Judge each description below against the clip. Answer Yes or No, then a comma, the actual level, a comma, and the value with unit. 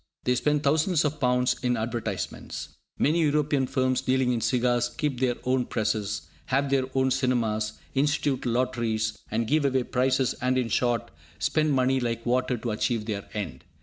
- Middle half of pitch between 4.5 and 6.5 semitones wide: No, narrow, 2.4 semitones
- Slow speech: No, average, 165 wpm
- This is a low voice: Yes, low, 125 Hz